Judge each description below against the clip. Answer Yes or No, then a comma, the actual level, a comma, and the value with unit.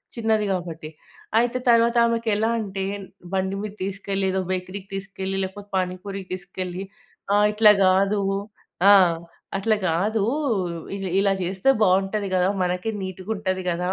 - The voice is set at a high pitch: Yes, high, 195 Hz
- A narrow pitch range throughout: Yes, narrow, 2.1 semitones